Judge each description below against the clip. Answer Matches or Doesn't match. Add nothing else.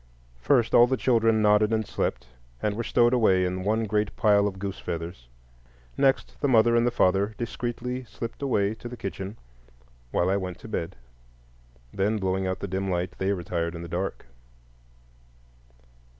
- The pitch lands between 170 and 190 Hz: Doesn't match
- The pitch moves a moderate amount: Matches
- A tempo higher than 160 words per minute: Matches